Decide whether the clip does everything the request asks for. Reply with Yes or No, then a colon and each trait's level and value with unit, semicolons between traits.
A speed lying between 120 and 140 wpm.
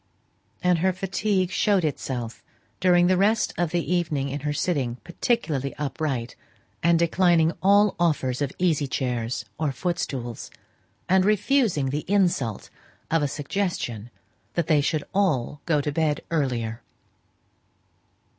Yes: slow, 135 wpm